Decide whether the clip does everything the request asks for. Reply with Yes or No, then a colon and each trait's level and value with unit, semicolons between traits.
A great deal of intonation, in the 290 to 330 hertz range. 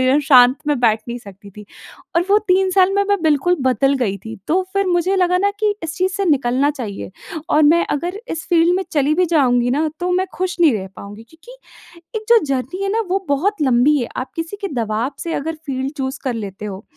Yes: wide, 6.7 semitones; very high, 295 Hz